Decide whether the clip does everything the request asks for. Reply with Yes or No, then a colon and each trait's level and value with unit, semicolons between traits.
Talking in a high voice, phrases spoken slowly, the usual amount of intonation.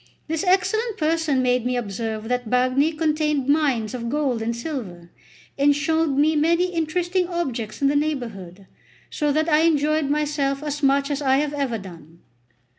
No: very high, 285 Hz; average, 170 wpm; average, 4.1 semitones